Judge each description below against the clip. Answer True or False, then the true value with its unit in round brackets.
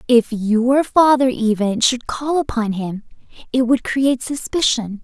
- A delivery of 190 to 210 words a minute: False (145 wpm)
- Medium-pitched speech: False (245 Hz)